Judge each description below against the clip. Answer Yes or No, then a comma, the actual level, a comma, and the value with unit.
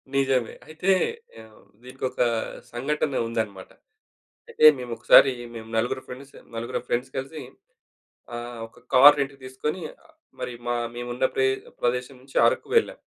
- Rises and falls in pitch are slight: Yes, narrow, 2.3 semitones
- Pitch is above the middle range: No, low, 130 Hz